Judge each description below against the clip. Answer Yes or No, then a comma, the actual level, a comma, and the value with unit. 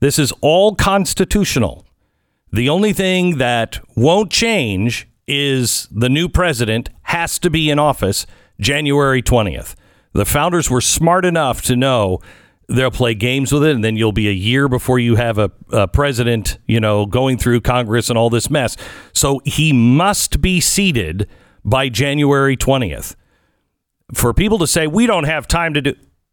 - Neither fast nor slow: Yes, average, 165 wpm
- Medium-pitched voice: No, low, 130 Hz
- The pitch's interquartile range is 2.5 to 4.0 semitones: No, average, 5.2 semitones